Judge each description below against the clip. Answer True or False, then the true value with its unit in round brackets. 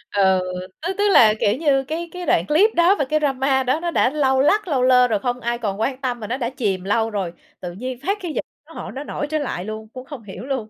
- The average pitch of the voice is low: False (255 Hz)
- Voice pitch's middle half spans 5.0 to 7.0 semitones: True (5.3 semitones)